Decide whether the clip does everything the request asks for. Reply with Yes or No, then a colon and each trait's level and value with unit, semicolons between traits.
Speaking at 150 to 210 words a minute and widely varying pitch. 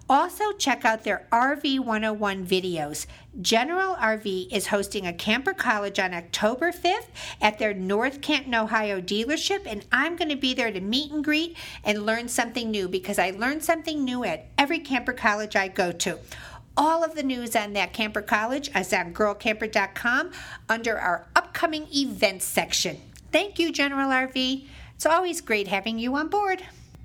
Yes: average, 170 wpm; wide, 6.3 semitones